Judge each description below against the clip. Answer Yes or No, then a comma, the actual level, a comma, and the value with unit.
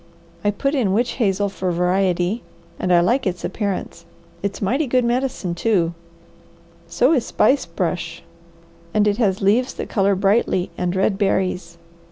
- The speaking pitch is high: Yes, high, 195 Hz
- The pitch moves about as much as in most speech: Yes, average, 4.2 semitones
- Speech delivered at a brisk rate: No, average, 155 wpm